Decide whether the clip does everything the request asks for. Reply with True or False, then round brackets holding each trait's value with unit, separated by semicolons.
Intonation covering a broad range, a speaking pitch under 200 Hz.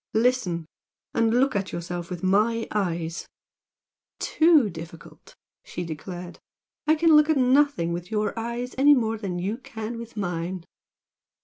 False (6.0 semitones; 215 Hz)